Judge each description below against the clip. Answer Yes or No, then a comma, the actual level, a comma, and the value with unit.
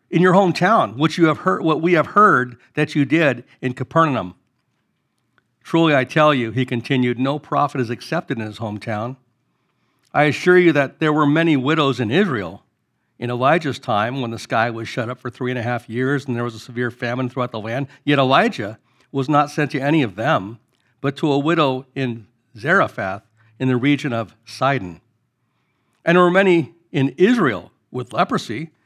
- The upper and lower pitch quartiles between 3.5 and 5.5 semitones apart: Yes, average, 4.0 semitones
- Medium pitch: No, low, 130 Hz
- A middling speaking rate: Yes, average, 190 wpm